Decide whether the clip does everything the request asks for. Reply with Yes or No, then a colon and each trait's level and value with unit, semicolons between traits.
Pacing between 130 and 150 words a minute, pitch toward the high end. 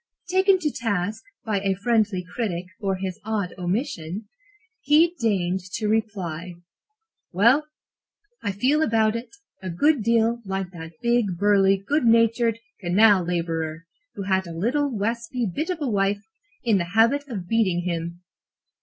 Yes: average, 145 wpm; high, 205 Hz